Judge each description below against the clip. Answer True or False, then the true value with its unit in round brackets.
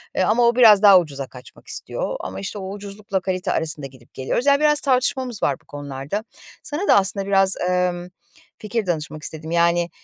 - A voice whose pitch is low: False (190 Hz)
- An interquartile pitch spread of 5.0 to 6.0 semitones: True (5.5 semitones)